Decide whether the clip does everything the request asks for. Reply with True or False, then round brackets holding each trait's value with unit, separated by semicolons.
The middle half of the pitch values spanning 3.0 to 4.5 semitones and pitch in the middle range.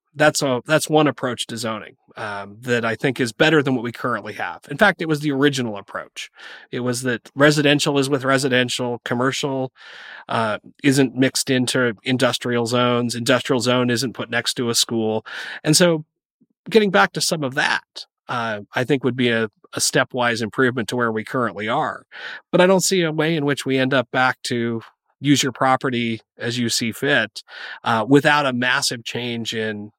False (3.4 semitones; 130 Hz)